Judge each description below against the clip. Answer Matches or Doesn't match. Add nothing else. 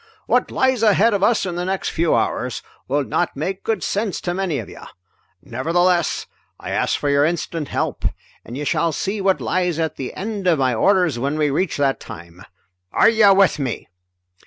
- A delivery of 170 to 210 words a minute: Matches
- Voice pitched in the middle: Matches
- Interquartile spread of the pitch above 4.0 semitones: Matches